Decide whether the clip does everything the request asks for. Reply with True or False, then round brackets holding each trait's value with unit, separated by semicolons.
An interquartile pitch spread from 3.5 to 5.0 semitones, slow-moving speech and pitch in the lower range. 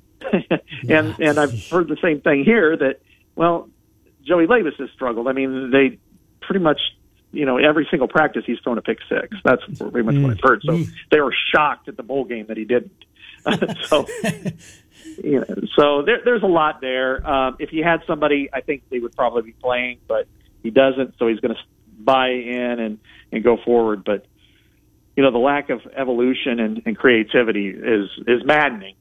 False (4.7 semitones; 190 wpm; 130 Hz)